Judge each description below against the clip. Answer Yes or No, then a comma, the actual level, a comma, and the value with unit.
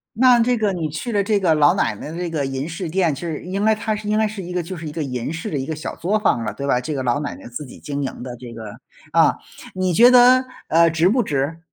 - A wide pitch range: Yes, wide, 6.6 semitones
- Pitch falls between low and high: Yes, medium, 165 Hz